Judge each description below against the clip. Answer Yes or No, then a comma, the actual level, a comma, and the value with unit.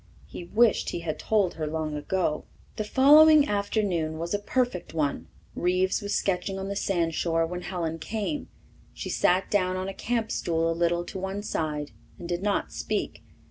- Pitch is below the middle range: No, medium, 185 Hz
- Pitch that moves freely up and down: No, average, 3.7 semitones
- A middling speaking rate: Yes, average, 180 wpm